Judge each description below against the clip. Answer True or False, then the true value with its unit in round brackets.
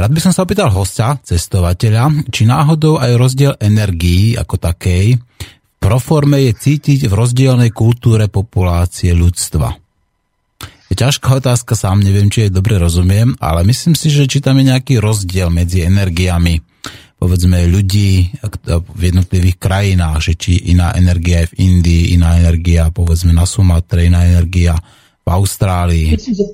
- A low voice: True (100 Hz)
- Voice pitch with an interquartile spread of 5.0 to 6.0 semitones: True (5.5 semitones)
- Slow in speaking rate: False (145 wpm)